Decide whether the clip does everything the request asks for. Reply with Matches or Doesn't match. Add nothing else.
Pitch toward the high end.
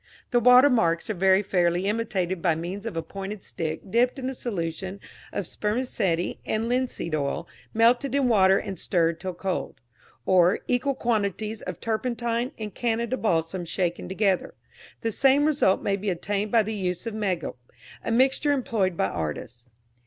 Matches